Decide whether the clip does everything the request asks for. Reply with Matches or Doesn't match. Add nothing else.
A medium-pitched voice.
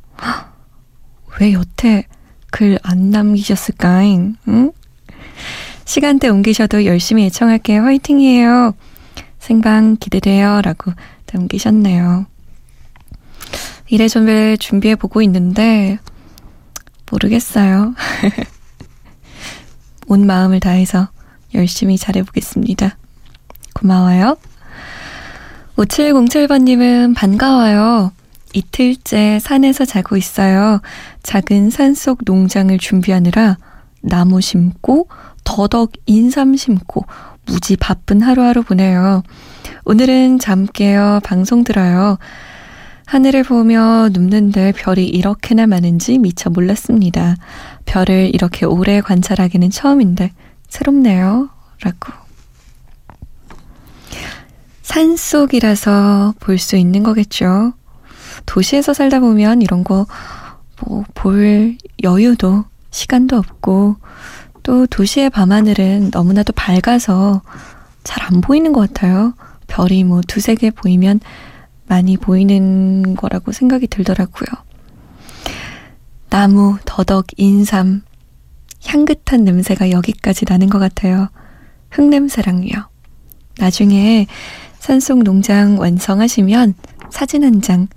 Doesn't match